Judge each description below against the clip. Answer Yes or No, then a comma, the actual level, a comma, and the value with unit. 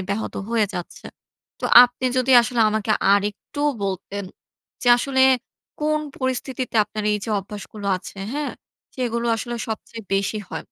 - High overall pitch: Yes, high, 225 Hz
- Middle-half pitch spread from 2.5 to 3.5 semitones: No, average, 3.9 semitones